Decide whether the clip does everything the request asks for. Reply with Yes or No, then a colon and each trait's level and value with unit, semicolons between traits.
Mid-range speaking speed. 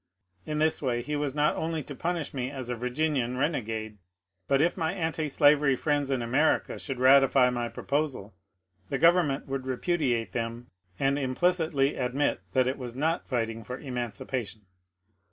Yes: average, 165 wpm